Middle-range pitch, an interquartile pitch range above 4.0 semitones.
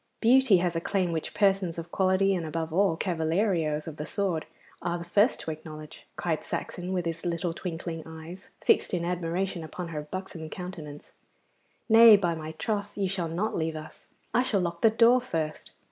No: medium, 175 Hz; average, 3.2 semitones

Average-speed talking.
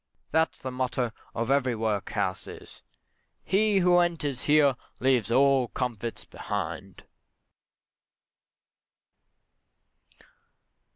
No: slow, 80 wpm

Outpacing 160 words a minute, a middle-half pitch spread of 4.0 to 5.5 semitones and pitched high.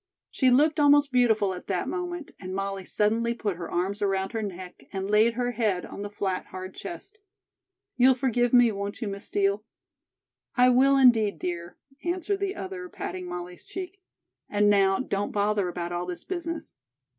Yes: average, 175 wpm; average, 5.1 semitones; high, 210 Hz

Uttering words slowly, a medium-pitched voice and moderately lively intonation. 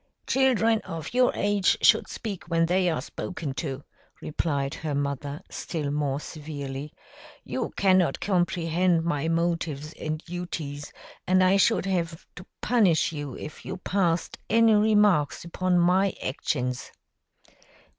Yes: slow, 130 wpm; medium, 170 Hz; average, 4.2 semitones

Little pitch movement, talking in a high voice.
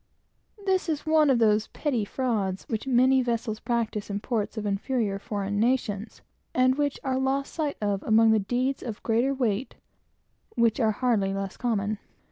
No: average, 4.0 semitones; high, 230 Hz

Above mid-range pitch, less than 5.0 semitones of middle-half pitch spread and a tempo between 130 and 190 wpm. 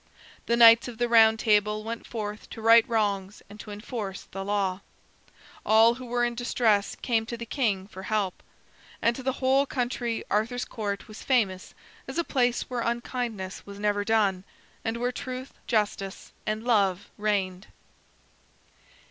Yes: high, 220 Hz; average, 2.8 semitones; average, 160 wpm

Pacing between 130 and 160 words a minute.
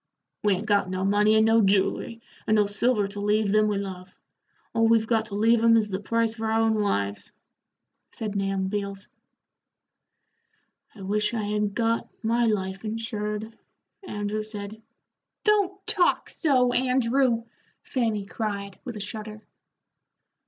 Yes: average, 150 wpm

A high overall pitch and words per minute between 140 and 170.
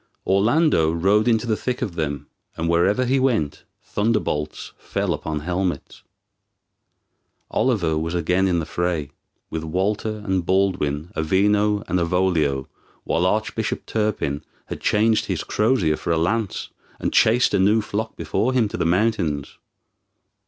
No: very low, 95 Hz; average, 145 wpm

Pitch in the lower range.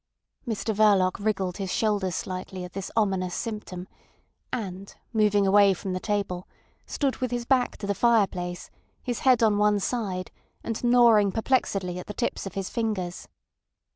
No: high, 205 Hz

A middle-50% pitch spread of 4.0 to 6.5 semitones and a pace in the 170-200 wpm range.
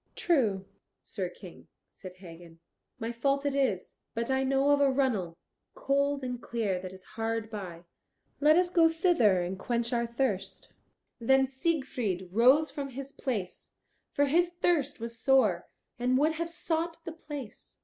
No: average, 5.3 semitones; average, 160 wpm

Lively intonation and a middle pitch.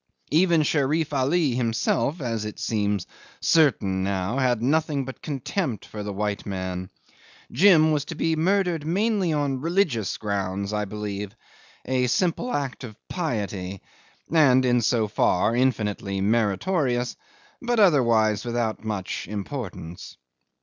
No: wide, 6.9 semitones; low, 120 Hz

